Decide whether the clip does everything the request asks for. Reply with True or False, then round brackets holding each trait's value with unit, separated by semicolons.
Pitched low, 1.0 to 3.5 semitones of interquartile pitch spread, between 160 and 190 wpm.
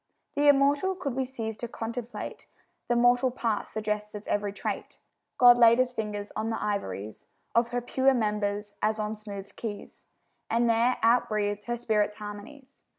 False (225 Hz; 2.8 semitones; 165 wpm)